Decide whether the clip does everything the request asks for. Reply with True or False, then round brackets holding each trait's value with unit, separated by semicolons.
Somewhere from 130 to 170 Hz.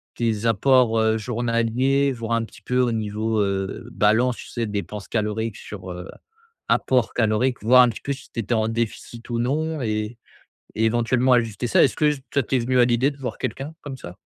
False (115 Hz)